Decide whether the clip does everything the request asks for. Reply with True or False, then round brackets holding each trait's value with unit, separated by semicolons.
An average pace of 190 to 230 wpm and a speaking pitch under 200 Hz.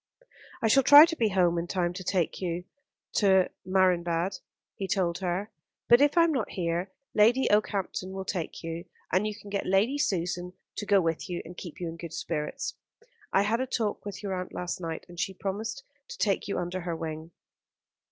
True (200 wpm; 185 Hz)